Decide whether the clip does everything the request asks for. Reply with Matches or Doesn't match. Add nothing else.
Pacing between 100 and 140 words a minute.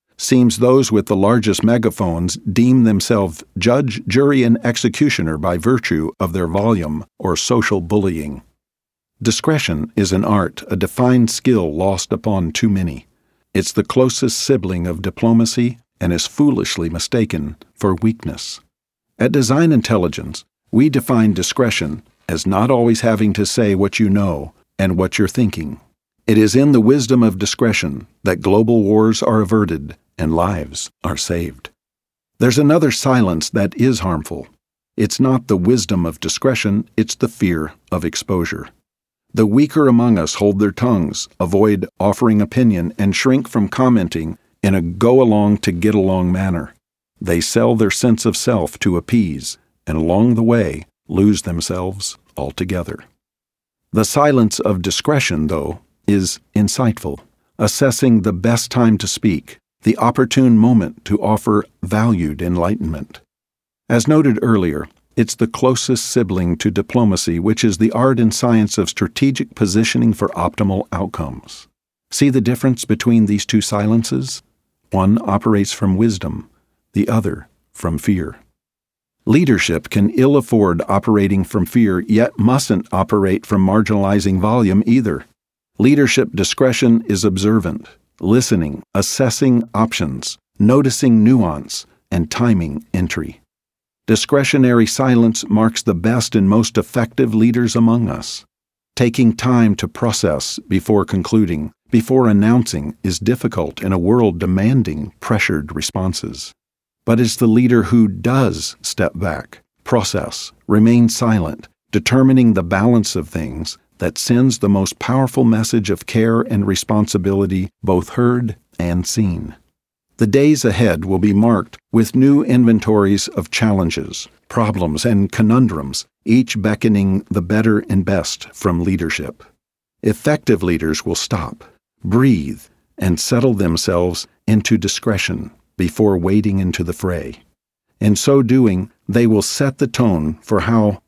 Matches